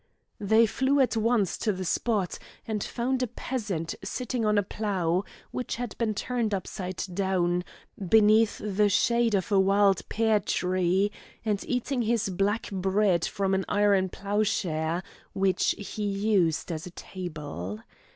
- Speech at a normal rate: Yes, average, 145 wpm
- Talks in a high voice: Yes, high, 200 Hz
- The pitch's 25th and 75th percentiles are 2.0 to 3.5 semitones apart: Yes, average, 3.0 semitones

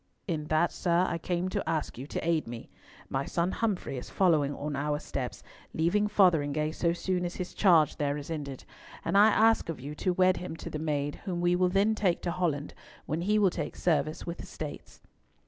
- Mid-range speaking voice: Yes, medium, 170 Hz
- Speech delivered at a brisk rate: Yes, fast, 215 wpm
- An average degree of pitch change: Yes, average, 3.5 semitones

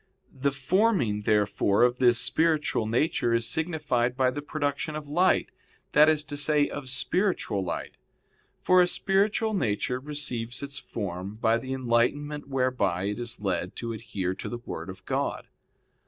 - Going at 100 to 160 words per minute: Yes, average, 155 wpm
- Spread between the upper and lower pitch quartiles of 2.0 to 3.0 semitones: No, average, 4.8 semitones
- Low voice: Yes, low, 130 Hz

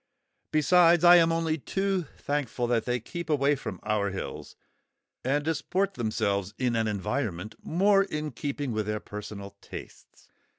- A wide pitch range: Yes, wide, 7.5 semitones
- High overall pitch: No, medium, 140 Hz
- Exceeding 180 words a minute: No, average, 145 wpm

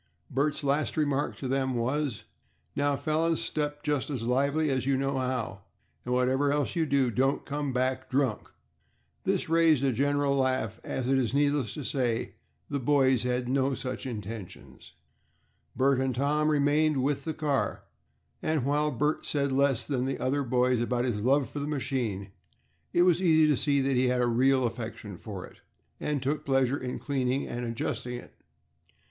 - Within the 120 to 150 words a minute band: No, average, 175 wpm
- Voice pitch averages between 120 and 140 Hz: Yes, low, 135 Hz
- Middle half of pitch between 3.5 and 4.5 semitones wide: No, narrow, 2.5 semitones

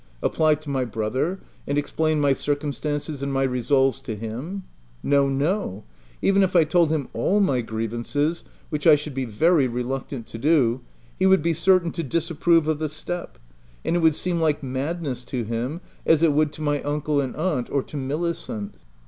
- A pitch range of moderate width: Yes, average, 3.8 semitones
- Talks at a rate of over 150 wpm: Yes, average, 180 wpm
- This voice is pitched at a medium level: Yes, medium, 145 Hz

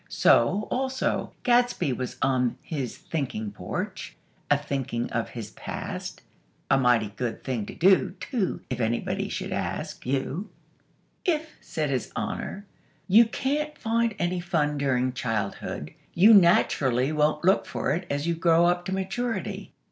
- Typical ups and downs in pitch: No, wide, 7.3 semitones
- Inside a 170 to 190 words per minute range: No, average, 145 wpm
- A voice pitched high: No, medium, 155 Hz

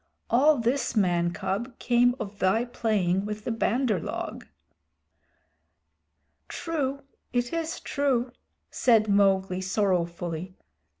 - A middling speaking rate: No, slow, 105 wpm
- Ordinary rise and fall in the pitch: Yes, average, 4.5 semitones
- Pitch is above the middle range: Yes, high, 220 Hz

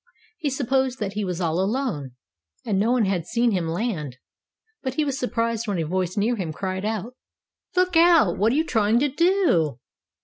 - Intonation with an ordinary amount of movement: No, wide, 6.1 semitones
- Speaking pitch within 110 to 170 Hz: No, high, 220 Hz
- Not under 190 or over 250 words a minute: Yes, average, 195 wpm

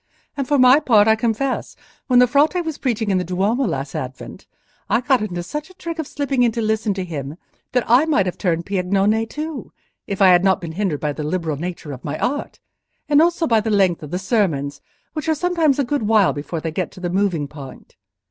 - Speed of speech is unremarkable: No, fast, 235 wpm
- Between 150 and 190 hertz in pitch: No, high, 210 Hz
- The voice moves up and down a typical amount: No, wide, 7.3 semitones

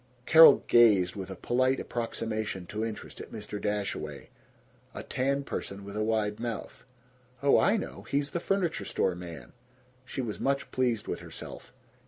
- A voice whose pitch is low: Yes, low, 115 Hz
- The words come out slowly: No, average, 160 wpm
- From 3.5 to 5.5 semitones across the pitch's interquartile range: Yes, average, 4.6 semitones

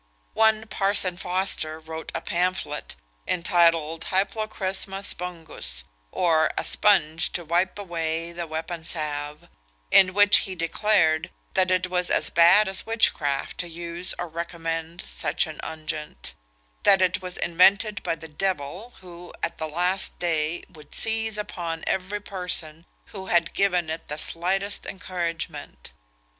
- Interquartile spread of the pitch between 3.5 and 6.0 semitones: No, average, 2.9 semitones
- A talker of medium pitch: Yes, medium, 175 Hz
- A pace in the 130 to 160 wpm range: Yes, slow, 135 wpm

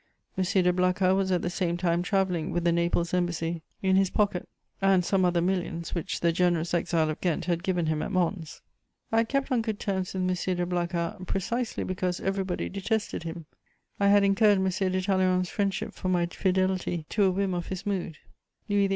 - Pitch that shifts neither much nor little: No, narrow, 2.0 semitones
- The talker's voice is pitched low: No, medium, 185 Hz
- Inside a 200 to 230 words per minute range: Yes, fast, 205 wpm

